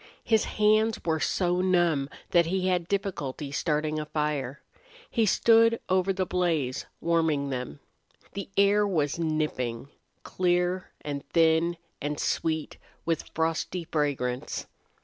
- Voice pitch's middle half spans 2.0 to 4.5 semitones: Yes, average, 3.9 semitones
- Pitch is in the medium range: Yes, medium, 165 Hz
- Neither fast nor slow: No, slow, 125 wpm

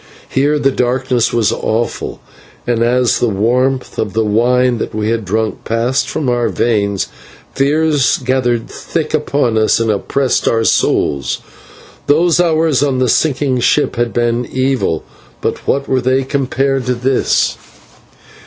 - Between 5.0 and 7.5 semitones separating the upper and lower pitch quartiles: No, average, 2.8 semitones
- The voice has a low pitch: Yes, low, 125 Hz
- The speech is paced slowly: No, average, 145 wpm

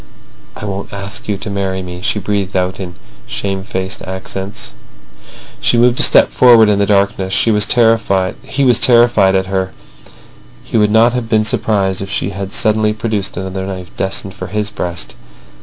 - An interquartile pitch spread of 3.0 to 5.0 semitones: No, narrow, 2.4 semitones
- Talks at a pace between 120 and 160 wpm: No, average, 170 wpm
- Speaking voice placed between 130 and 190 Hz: No, low, 100 Hz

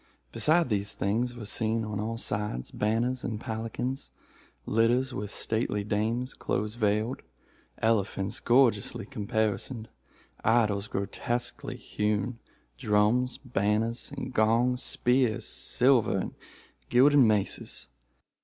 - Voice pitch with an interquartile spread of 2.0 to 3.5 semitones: Yes, average, 2.7 semitones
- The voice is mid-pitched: No, low, 110 Hz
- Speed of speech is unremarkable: No, slow, 105 wpm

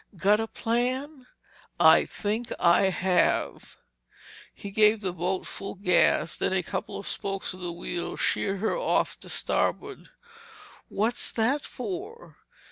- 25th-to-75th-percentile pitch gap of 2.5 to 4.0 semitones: No, average, 4.7 semitones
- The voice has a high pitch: Yes, high, 205 Hz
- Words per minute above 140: No, slow, 135 wpm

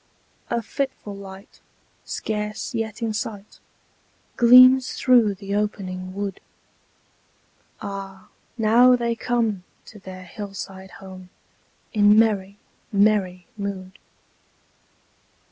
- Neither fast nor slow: No, slow, 95 wpm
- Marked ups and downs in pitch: No, average, 2.7 semitones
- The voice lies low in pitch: No, high, 205 Hz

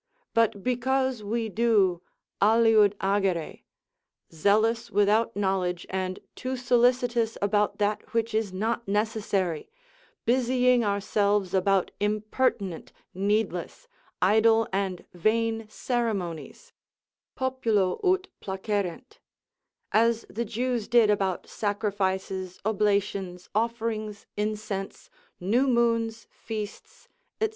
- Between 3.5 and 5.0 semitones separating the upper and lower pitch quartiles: No, average, 2.9 semitones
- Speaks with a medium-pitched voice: No, high, 215 Hz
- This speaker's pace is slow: Yes, slow, 95 wpm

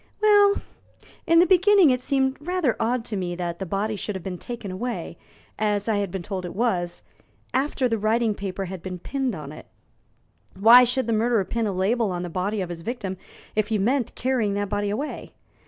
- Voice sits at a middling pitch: No, high, 215 Hz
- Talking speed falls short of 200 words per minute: No, fast, 205 wpm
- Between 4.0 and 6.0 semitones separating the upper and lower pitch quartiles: Yes, average, 4.7 semitones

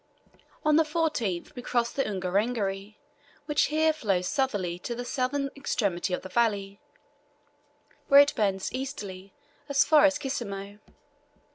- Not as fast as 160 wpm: Yes, slow, 135 wpm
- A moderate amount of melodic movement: No, wide, 6.2 semitones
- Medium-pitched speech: No, high, 235 Hz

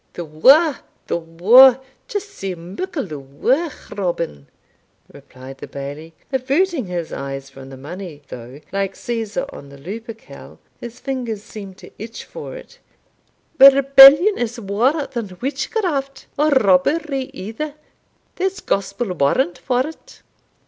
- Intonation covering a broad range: Yes, wide, 8.2 semitones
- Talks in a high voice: Yes, high, 225 Hz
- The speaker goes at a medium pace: No, slow, 130 wpm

